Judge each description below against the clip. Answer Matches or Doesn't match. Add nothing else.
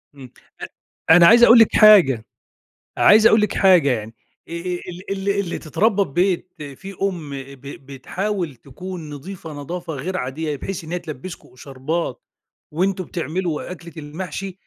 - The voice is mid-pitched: Matches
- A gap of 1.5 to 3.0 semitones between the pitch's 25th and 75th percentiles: Doesn't match